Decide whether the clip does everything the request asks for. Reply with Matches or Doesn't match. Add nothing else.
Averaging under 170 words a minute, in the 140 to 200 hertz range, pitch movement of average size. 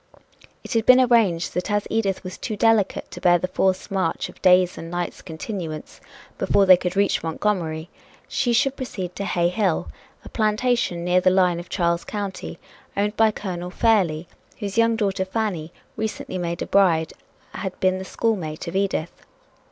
Doesn't match